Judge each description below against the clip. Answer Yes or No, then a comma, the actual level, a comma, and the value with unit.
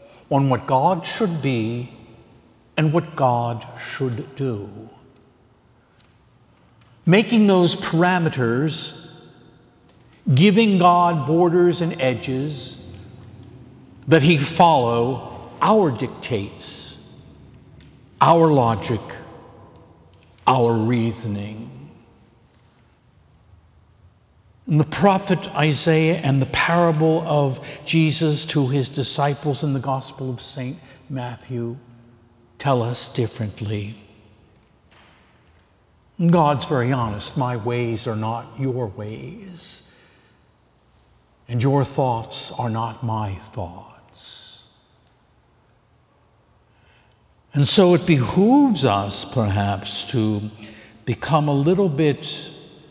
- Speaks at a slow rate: Yes, slow, 85 wpm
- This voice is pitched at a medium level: No, low, 130 Hz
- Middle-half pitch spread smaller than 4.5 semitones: No, wide, 5.4 semitones